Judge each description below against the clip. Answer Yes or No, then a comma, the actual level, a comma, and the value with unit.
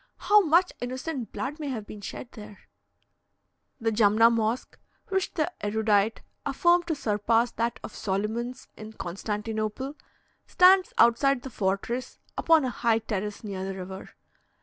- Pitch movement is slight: No, average, 4.4 semitones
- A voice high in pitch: Yes, high, 230 Hz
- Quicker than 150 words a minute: No, average, 140 wpm